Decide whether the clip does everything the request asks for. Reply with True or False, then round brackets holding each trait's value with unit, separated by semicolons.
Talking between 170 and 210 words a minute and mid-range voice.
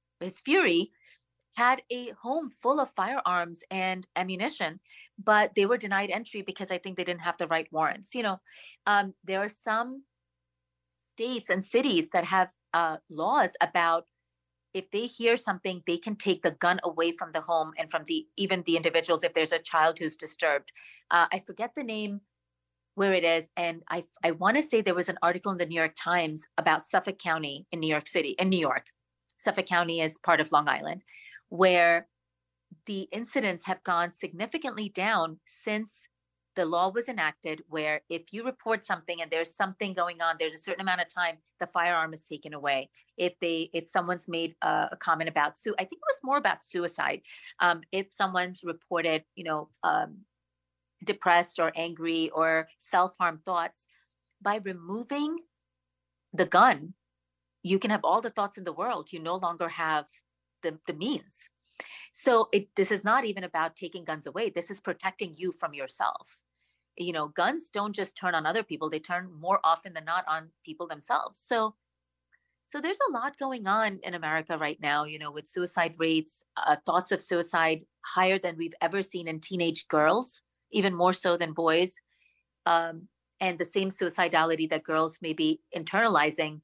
True (180 wpm; 175 Hz)